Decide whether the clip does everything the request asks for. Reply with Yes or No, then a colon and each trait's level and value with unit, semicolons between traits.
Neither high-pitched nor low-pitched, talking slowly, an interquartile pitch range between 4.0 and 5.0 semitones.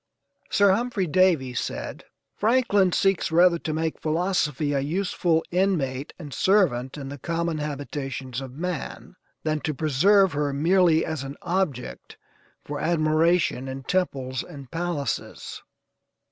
Yes: medium, 160 Hz; slow, 130 wpm; average, 4.6 semitones